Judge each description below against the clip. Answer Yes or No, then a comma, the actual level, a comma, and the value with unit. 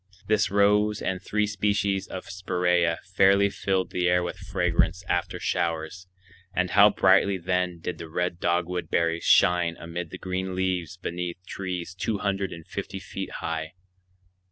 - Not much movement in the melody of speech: Yes, narrow, 1.8 semitones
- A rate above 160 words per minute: No, average, 155 wpm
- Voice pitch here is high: No, very low, 90 Hz